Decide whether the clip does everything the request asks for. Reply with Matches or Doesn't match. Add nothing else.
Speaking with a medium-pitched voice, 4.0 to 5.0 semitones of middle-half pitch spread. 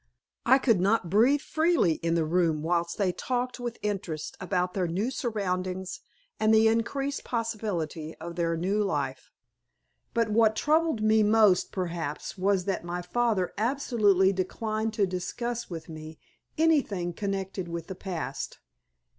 Doesn't match